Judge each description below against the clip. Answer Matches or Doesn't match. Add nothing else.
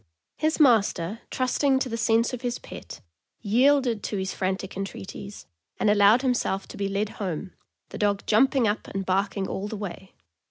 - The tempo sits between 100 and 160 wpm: Doesn't match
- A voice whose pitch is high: Matches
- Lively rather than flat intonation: Doesn't match